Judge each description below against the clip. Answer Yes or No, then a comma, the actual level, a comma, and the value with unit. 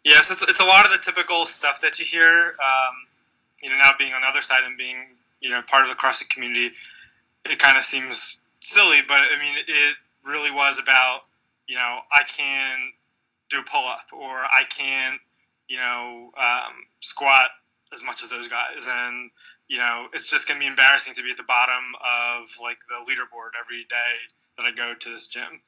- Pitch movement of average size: No, narrow, 2.2 semitones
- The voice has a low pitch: Yes, low, 130 Hz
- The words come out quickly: Yes, fast, 210 wpm